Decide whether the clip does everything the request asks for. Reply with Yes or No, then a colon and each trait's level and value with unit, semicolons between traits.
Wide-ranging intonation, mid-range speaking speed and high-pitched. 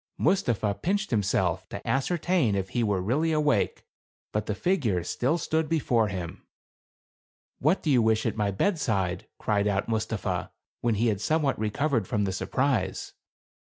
No: wide, 6.8 semitones; average, 165 wpm; low, 110 Hz